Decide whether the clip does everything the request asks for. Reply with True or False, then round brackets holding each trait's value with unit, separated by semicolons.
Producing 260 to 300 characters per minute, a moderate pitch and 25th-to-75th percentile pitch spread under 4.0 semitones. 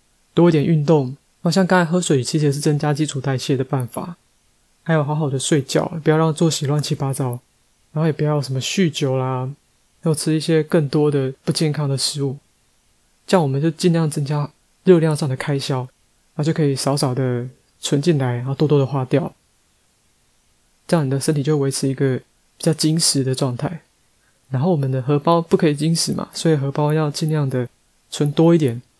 True (290 characters per minute; 150 Hz; 2.9 semitones)